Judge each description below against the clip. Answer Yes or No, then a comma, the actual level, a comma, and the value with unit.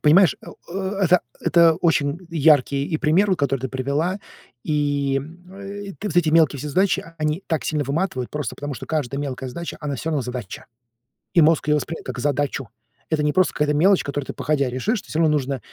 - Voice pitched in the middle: Yes, medium, 150 Hz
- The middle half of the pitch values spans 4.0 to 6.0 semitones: No, average, 3.2 semitones